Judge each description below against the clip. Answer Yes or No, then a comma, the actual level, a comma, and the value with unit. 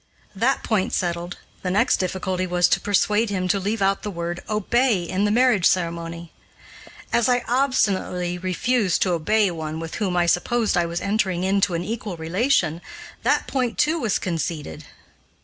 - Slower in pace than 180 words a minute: Yes, average, 165 wpm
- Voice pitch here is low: No, high, 190 Hz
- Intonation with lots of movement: No, average, 3.8 semitones